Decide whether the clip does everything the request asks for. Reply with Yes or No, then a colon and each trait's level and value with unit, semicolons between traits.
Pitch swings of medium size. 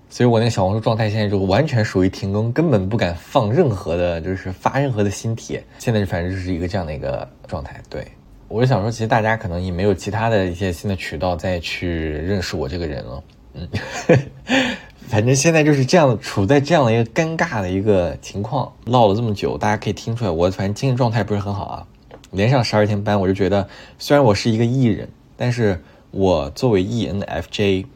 Yes: average, 3.9 semitones